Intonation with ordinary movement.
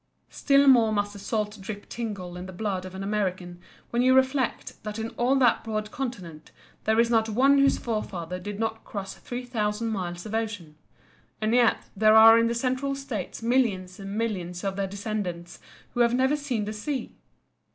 Yes: average, 3.6 semitones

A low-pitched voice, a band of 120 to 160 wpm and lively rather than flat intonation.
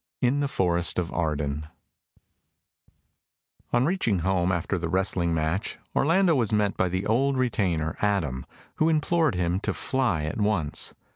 Yes: very low, 95 Hz; average, 145 wpm; wide, 6.9 semitones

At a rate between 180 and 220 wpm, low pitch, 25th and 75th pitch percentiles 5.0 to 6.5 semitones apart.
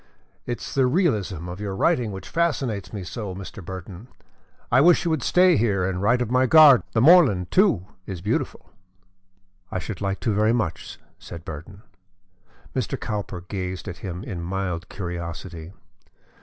No: average, 165 wpm; low, 100 Hz; average, 5.3 semitones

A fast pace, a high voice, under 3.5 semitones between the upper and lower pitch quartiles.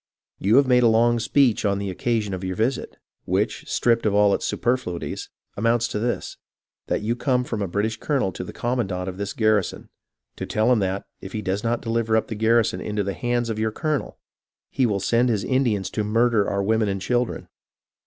No: fast, 220 wpm; low, 110 Hz; average, 3.1 semitones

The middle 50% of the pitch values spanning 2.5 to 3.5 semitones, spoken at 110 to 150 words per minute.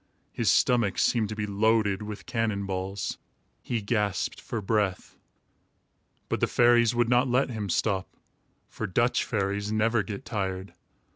Yes: average, 2.8 semitones; average, 145 wpm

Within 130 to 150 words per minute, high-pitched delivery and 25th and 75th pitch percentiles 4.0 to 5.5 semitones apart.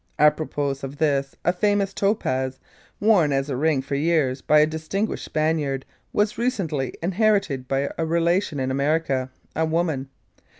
No: average, 145 wpm; medium, 155 Hz; average, 4.3 semitones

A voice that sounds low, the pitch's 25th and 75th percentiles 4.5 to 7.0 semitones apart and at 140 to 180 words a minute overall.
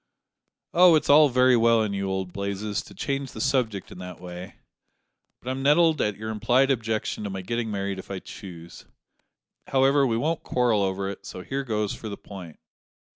No: low, 110 Hz; average, 5.3 semitones; average, 190 wpm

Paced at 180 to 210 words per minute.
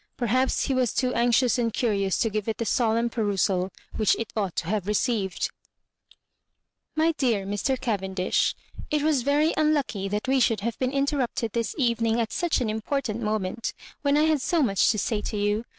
Yes: average, 190 wpm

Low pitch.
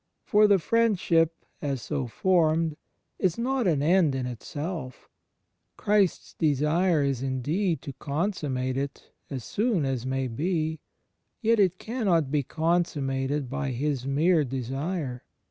No: medium, 155 Hz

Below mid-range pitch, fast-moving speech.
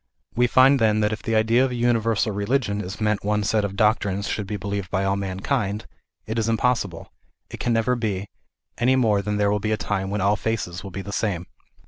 Yes: low, 105 Hz; fast, 240 wpm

